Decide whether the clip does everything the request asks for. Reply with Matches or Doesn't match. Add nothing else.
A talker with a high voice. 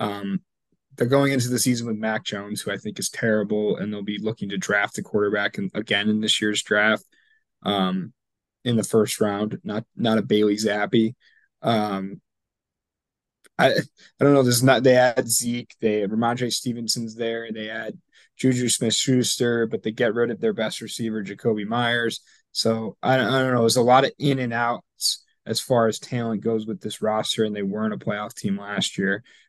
Doesn't match